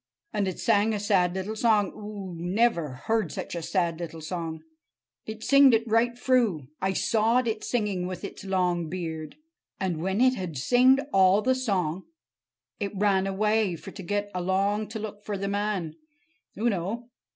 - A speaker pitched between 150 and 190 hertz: No, high, 200 Hz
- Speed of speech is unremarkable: Yes, average, 170 wpm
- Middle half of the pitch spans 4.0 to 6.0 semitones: No, average, 3.5 semitones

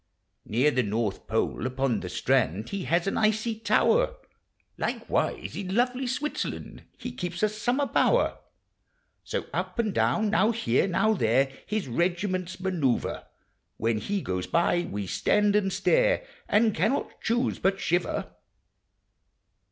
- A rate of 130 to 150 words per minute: Yes, average, 140 wpm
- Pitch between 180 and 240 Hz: Yes, high, 190 Hz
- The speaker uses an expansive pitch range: Yes, wide, 8.6 semitones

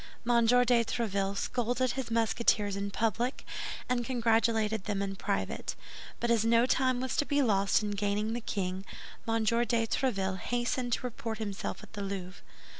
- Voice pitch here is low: No, high, 225 Hz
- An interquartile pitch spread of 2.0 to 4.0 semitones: Yes, average, 3.1 semitones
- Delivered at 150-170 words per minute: Yes, average, 165 wpm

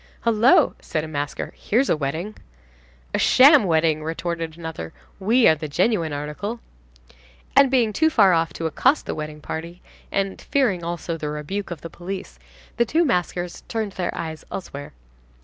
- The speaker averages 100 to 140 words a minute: No, average, 165 wpm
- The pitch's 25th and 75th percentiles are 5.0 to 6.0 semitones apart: Yes, wide, 5.6 semitones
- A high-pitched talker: No, medium, 175 Hz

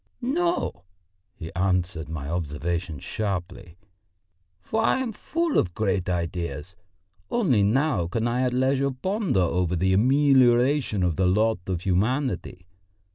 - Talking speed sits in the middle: No, slow, 130 wpm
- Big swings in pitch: Yes, wide, 7.0 semitones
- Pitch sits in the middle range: No, very low, 95 Hz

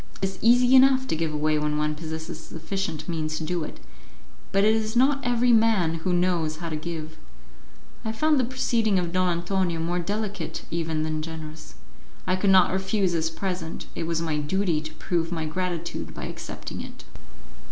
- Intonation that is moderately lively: Yes, average, 4.1 semitones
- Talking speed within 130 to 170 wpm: No, average, 185 wpm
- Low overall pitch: No, medium, 175 Hz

